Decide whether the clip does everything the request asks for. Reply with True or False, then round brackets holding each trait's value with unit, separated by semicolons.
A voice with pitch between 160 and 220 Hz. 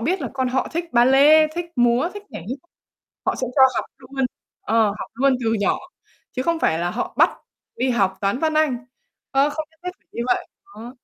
False (260 Hz)